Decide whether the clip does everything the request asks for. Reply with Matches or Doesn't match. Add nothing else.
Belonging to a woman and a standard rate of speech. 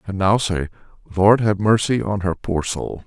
Doesn't match